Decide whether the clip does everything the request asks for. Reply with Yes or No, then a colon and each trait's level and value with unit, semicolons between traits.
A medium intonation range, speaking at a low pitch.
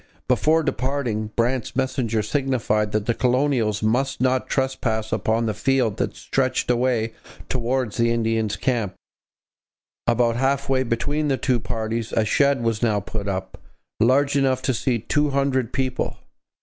Yes: average, 3.1 semitones; low, 125 Hz